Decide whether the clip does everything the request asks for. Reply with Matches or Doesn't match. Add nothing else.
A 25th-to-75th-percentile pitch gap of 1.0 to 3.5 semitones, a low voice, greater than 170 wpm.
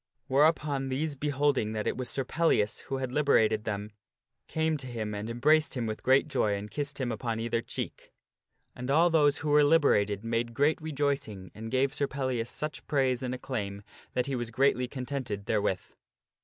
Doesn't match